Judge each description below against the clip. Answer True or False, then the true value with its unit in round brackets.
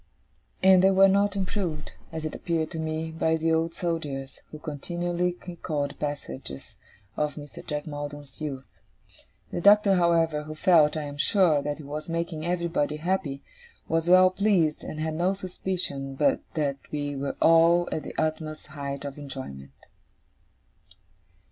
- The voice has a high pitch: False (160 Hz)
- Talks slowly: False (155 wpm)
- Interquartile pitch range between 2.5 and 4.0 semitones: True (3.0 semitones)